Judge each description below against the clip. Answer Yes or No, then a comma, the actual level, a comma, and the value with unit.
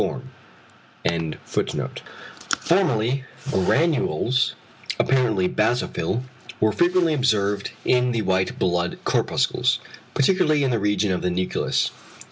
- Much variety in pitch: Yes, wide, 6.0 semitones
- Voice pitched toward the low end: Yes, low, 115 Hz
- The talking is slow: Yes, slow, 95 wpm